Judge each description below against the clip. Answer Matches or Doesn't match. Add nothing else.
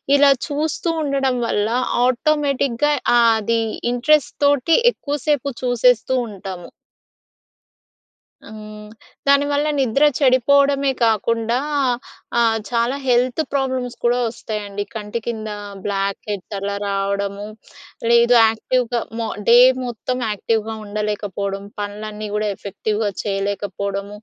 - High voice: Matches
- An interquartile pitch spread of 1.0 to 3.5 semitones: Doesn't match